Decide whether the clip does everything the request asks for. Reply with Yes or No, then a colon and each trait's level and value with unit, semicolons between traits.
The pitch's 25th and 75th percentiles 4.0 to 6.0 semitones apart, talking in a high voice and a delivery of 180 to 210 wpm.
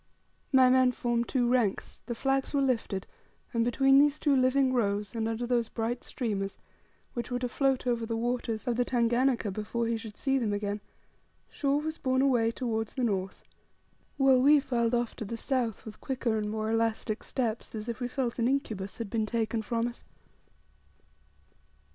No: narrow, 2.6 semitones; high, 235 Hz; average, 185 wpm